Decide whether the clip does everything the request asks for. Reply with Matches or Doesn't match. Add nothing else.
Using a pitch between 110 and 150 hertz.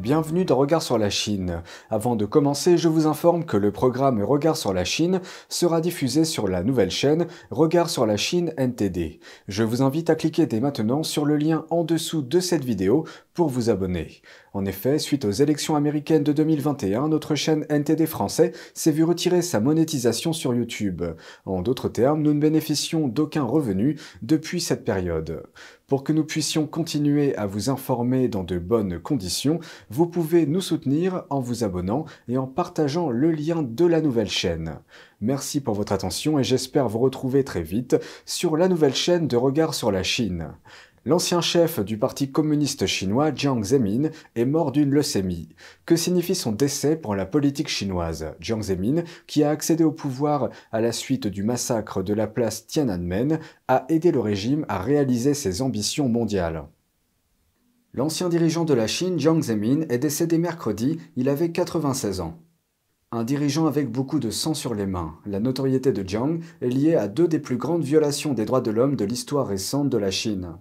Matches